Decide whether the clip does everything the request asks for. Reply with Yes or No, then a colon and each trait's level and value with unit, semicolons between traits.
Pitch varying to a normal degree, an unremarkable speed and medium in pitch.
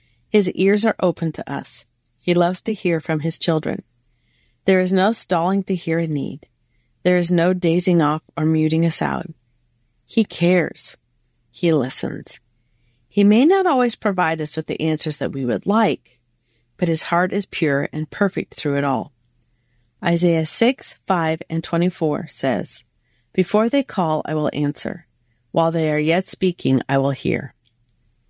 No: wide, 6.6 semitones; average, 165 wpm; medium, 160 Hz